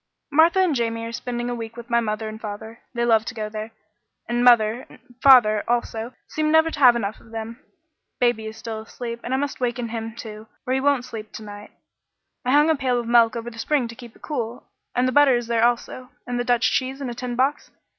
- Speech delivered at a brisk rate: Yes, fast, 240 wpm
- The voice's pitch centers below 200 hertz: No, high, 240 Hz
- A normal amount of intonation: No, narrow, 2.2 semitones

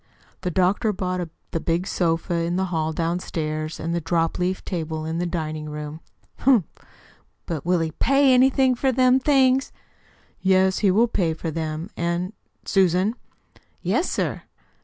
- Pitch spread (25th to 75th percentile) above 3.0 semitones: Yes, average, 3.7 semitones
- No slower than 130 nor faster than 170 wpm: Yes, average, 155 wpm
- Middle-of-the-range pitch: Yes, medium, 175 Hz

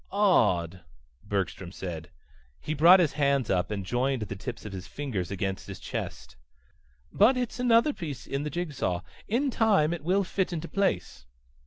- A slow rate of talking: No, average, 170 wpm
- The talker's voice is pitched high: No, medium, 140 Hz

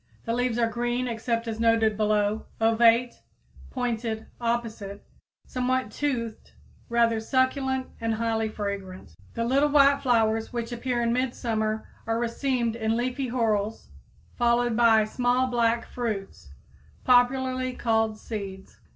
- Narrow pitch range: Yes, narrow, 2.0 semitones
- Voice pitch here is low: No, high, 230 Hz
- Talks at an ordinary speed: No, slow, 125 wpm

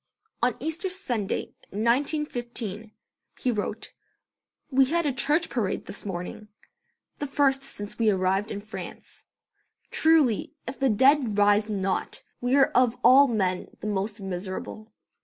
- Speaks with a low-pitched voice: No, high, 230 Hz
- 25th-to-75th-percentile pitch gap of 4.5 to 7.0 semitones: Yes, average, 4.9 semitones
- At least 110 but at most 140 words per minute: Yes, slow, 135 wpm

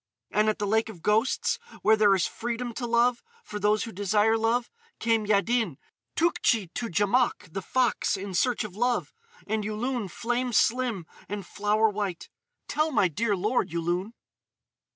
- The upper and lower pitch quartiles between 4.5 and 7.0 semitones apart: No, average, 3.0 semitones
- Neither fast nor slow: Yes, average, 160 wpm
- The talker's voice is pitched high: Yes, high, 220 Hz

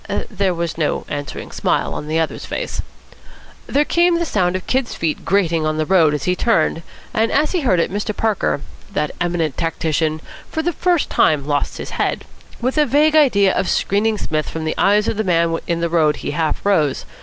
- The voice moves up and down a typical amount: No, wide, 6.0 semitones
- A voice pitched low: No, medium, 180 Hz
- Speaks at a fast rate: Yes, fast, 210 wpm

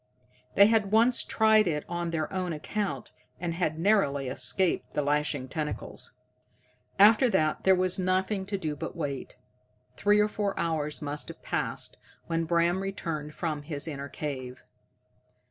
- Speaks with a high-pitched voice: No, medium, 170 Hz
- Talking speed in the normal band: Yes, average, 150 wpm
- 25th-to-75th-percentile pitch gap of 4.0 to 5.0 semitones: Yes, average, 4.7 semitones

